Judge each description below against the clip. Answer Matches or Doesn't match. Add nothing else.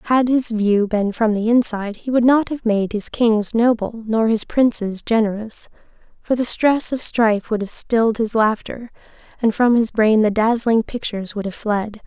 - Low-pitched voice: Doesn't match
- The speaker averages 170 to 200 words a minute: Matches